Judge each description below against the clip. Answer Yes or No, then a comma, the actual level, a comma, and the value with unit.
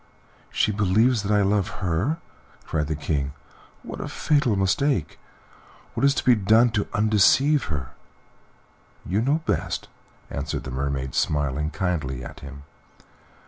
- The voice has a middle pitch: No, very low, 95 Hz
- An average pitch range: No, wide, 7.5 semitones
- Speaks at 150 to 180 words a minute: No, average, 140 wpm